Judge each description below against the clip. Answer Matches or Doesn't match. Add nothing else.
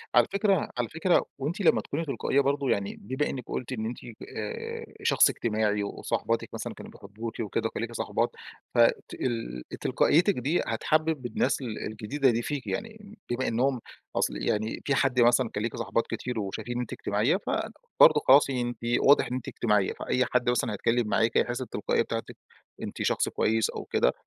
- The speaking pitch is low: Matches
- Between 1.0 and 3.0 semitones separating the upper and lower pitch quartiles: Doesn't match